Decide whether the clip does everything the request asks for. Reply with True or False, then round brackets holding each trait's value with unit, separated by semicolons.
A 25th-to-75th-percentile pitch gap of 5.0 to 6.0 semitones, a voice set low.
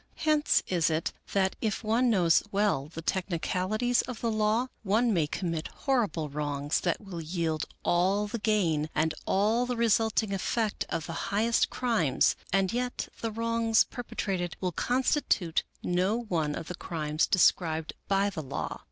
False (5.5 semitones; 195 Hz)